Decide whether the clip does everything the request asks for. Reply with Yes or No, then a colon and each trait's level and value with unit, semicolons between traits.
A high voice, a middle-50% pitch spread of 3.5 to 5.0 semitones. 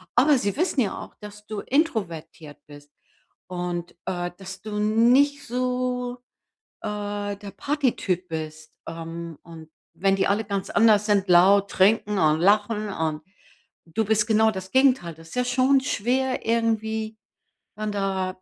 Yes: high, 205 Hz; average, 4.5 semitones